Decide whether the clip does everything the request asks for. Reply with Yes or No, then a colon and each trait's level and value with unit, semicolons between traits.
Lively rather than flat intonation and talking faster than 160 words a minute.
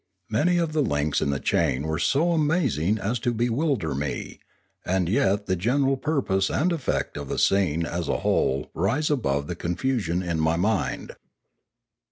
Yes: wide, 8.7 semitones; average, 175 wpm